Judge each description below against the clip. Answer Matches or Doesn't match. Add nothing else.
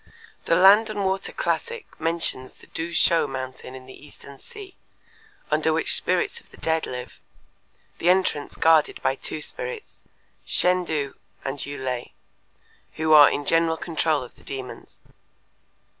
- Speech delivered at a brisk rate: Doesn't match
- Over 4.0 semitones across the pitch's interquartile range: Matches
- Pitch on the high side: Doesn't match